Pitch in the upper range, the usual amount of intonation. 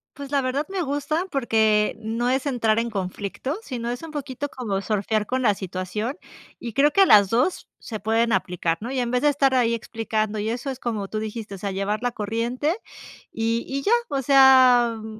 Yes: high, 235 Hz; average, 3.7 semitones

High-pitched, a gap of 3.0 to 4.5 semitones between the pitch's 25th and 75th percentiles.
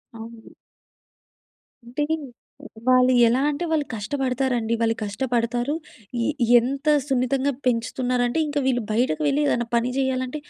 No: very high, 250 Hz; narrow, 2.5 semitones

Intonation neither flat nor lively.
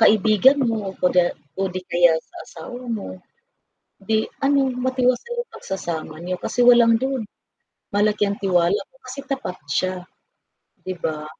No: wide, 5.7 semitones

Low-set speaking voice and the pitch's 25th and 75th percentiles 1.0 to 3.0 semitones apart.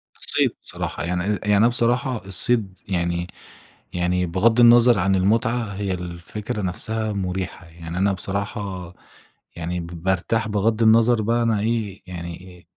No: low, 100 Hz; average, 3.9 semitones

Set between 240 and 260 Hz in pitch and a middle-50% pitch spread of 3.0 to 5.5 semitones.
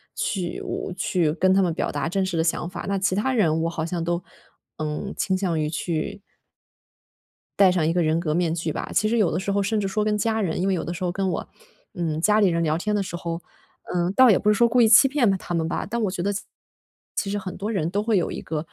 No: medium, 185 Hz; average, 3.5 semitones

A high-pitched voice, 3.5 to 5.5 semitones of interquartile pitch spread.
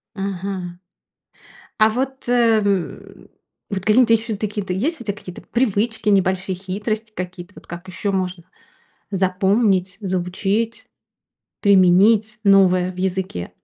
No: high, 195 Hz; average, 2.8 semitones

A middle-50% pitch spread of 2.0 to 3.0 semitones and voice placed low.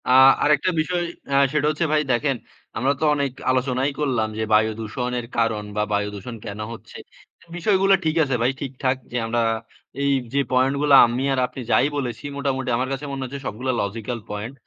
No: average, 3.4 semitones; low, 130 Hz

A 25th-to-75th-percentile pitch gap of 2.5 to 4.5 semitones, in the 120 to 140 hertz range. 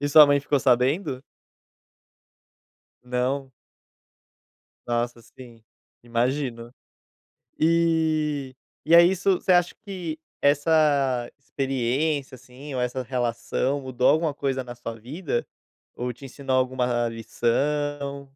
Yes: average, 3.2 semitones; low, 135 Hz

